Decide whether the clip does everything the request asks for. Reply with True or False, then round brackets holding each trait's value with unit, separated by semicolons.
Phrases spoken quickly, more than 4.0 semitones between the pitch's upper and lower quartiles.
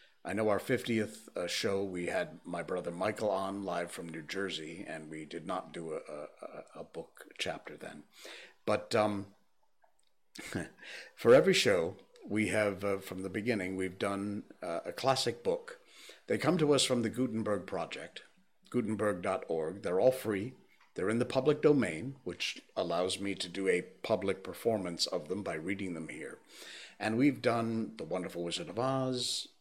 False (170 wpm; 4.7 semitones)